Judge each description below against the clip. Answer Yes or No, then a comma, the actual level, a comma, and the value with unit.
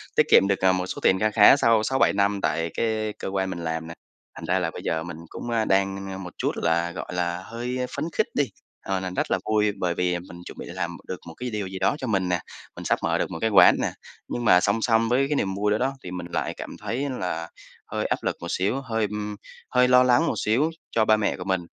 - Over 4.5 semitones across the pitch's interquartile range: No, average, 3.9 semitones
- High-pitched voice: No, low, 100 Hz